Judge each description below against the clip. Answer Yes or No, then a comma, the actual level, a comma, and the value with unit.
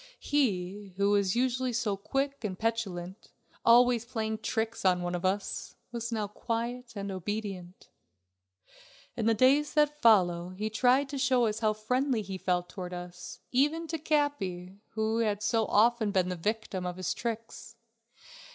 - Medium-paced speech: Yes, average, 160 wpm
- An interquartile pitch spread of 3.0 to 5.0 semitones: Yes, average, 4.3 semitones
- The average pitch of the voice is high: Yes, high, 220 Hz